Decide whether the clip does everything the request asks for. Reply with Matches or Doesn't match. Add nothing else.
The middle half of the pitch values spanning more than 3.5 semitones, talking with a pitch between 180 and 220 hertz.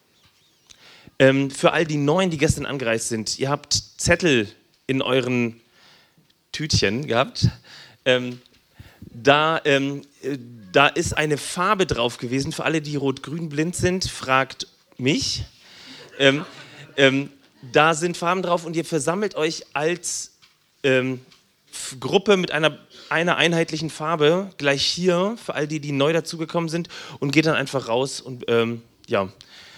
Doesn't match